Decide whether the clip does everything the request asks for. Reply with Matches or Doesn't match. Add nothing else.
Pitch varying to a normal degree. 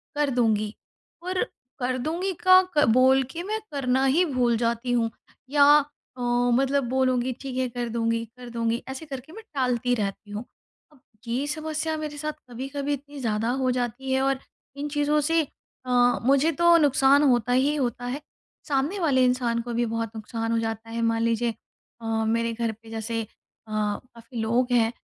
Matches